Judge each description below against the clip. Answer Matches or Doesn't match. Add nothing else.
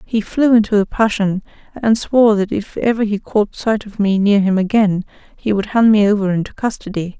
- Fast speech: Matches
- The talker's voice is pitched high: Matches